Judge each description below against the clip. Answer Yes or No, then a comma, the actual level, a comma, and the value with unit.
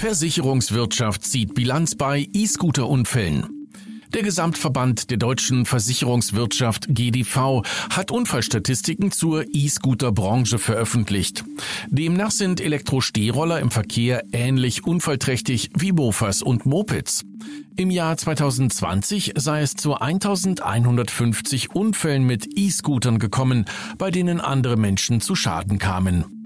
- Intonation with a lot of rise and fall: Yes, wide, 5.9 semitones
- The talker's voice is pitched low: Yes, low, 130 Hz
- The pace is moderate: No, slow, 100 wpm